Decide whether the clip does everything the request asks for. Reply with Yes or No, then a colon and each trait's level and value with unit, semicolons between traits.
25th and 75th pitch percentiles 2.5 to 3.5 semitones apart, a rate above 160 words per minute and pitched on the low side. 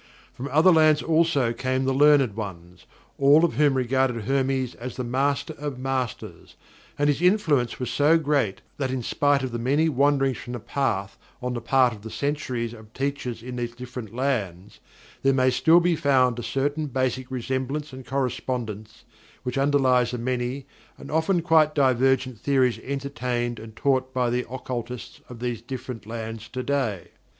Yes: average, 2.8 semitones; average, 170 wpm; low, 130 Hz